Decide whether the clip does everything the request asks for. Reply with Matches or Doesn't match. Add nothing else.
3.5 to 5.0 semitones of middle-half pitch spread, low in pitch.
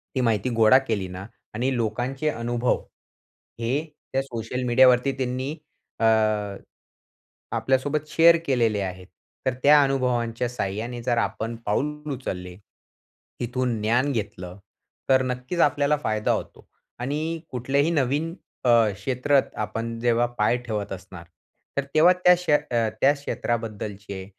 Matches